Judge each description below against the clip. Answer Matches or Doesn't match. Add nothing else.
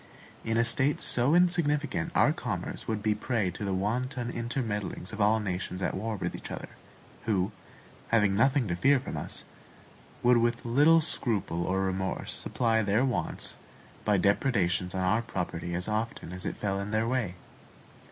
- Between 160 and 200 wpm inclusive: Matches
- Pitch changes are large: Doesn't match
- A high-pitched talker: Doesn't match